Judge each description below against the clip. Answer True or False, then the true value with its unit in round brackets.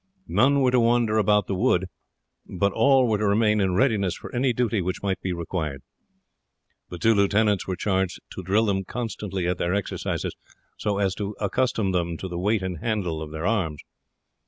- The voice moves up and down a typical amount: True (3.4 semitones)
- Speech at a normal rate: True (190 wpm)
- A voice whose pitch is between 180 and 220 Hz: False (100 Hz)